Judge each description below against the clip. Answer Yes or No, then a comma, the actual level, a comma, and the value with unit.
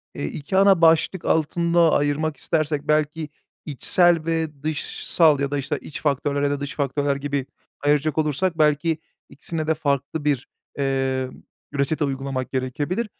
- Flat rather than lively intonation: Yes, narrow, 2.3 semitones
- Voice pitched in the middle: Yes, medium, 150 Hz